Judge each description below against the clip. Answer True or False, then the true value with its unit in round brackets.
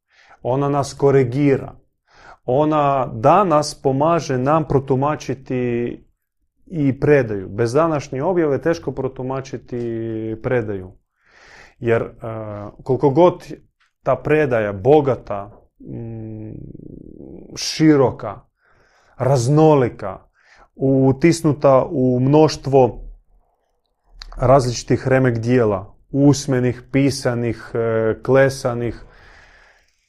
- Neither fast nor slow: False (65 wpm)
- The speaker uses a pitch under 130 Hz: False (135 Hz)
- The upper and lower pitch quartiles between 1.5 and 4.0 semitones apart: True (3.3 semitones)